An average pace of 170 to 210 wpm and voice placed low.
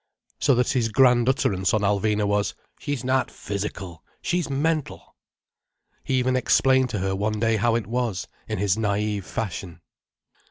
No: average, 155 wpm; low, 110 Hz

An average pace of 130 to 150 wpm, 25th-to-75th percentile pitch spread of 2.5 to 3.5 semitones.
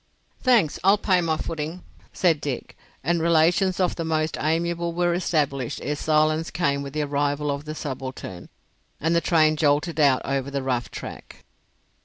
No: average, 165 wpm; average, 3.1 semitones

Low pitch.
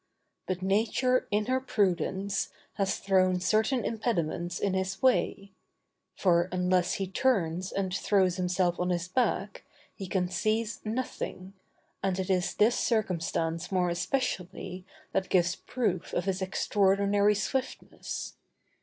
No: high, 190 Hz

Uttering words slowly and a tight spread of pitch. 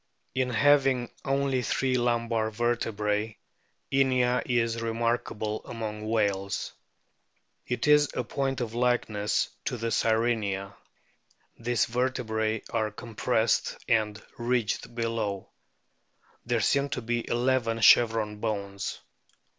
Yes: slow, 105 wpm; narrow, 2.3 semitones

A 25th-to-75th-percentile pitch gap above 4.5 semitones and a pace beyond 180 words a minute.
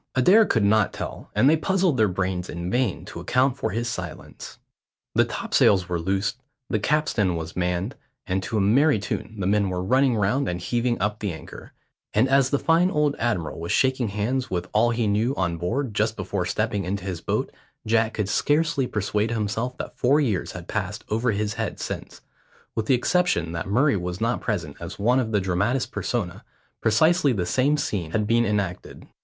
Yes: average, 5.2 semitones; average, 195 wpm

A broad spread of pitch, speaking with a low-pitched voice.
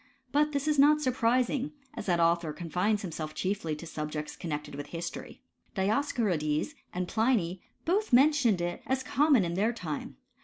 No: wide, 7.8 semitones; high, 200 Hz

